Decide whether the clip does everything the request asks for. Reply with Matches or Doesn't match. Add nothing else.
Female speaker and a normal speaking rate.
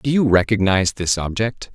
Doesn't match